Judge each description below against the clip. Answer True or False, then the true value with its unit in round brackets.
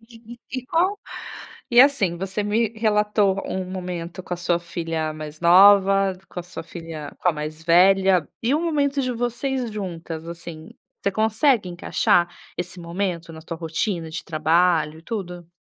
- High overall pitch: False (180 Hz)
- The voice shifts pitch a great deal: False (4.5 semitones)